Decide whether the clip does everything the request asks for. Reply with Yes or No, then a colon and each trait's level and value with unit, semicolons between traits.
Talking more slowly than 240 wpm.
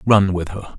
Yes: fast, 230 wpm